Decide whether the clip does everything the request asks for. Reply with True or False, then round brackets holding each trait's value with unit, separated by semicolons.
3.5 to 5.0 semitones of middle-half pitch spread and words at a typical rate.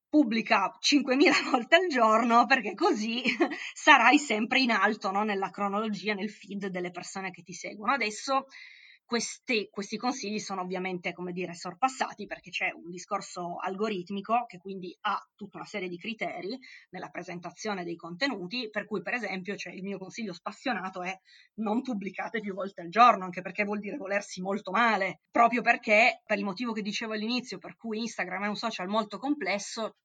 False (3.8 semitones; 175 wpm)